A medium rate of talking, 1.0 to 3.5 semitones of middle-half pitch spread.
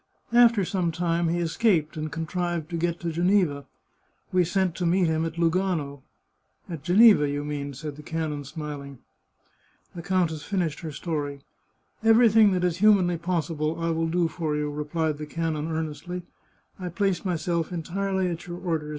Yes: average, 175 wpm; average, 2.9 semitones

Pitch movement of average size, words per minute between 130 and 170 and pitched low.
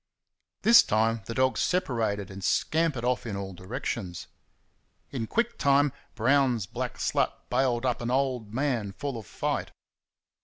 Yes: average, 4.1 semitones; average, 145 wpm; low, 120 Hz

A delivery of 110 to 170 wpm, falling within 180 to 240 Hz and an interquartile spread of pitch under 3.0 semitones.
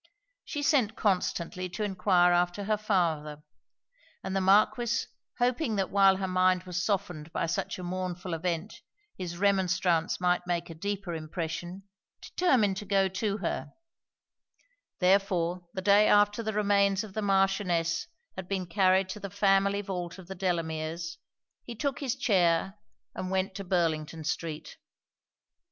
Yes: average, 145 wpm; high, 190 Hz; narrow, 2.6 semitones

